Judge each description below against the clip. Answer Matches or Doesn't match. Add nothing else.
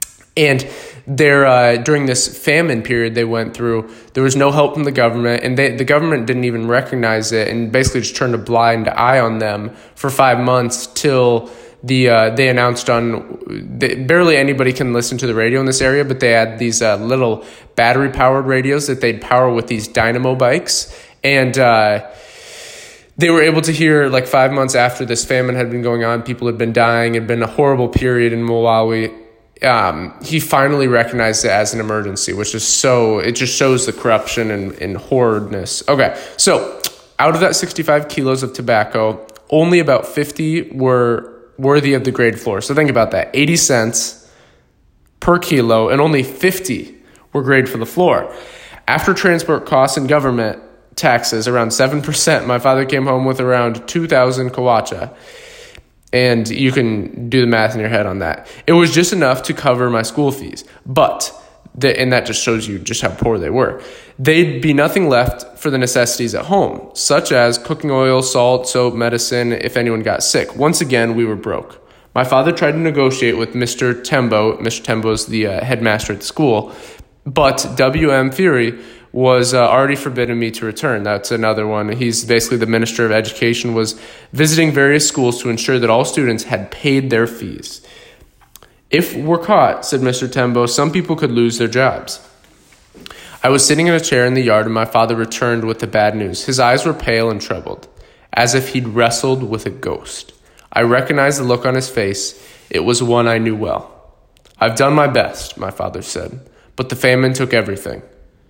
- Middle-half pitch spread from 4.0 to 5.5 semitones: Doesn't match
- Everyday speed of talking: Matches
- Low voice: Matches